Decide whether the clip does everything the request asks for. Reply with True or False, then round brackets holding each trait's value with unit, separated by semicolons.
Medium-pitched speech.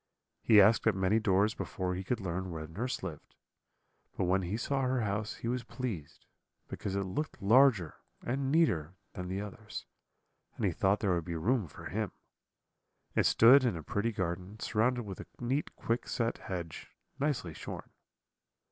False (105 Hz)